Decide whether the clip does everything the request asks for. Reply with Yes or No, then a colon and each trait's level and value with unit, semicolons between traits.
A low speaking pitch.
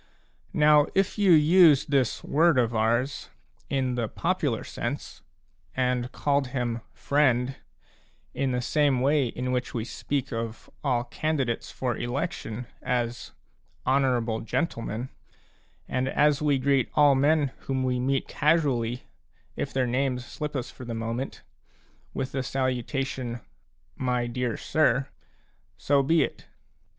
Yes: low, 130 Hz